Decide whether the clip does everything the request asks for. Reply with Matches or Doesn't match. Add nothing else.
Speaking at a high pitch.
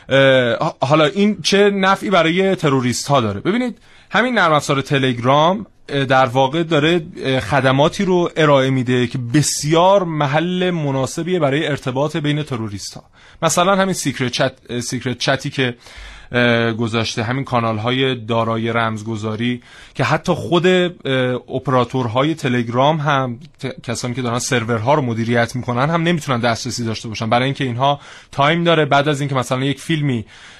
Doesn't match